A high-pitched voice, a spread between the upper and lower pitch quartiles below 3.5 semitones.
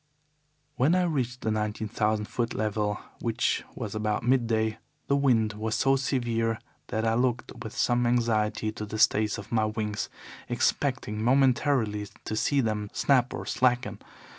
No: low, 115 Hz; average, 2.7 semitones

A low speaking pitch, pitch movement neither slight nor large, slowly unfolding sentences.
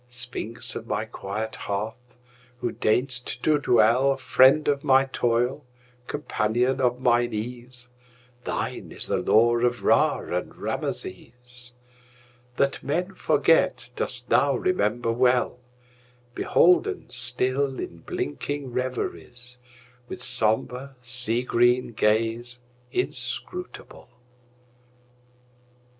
No: low, 125 Hz; narrow, 1.2 semitones; slow, 90 wpm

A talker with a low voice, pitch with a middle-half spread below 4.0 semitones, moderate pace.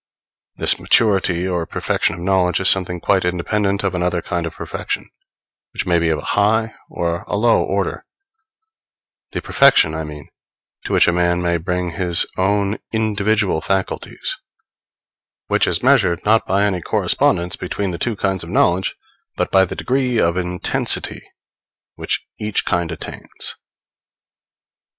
Yes: very low, 90 Hz; average, 2.8 semitones; average, 150 wpm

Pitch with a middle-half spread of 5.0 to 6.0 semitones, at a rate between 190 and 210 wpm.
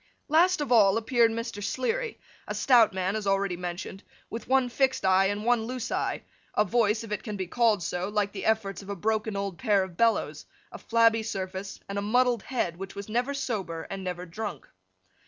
No: average, 3.3 semitones; fast, 205 wpm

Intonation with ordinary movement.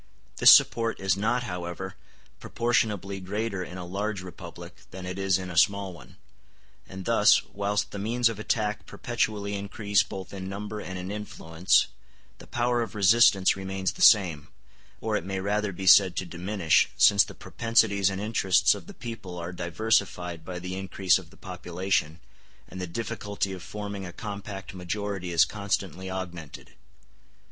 No: narrow, 2.3 semitones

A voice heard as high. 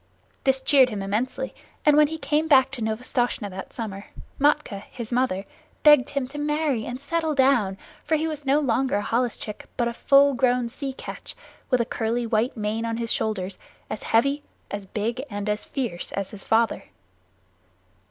Yes: high, 245 Hz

